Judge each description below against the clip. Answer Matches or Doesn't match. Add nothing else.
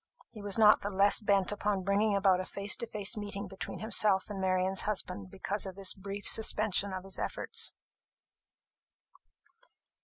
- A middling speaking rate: Matches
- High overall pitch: Matches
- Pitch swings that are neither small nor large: Doesn't match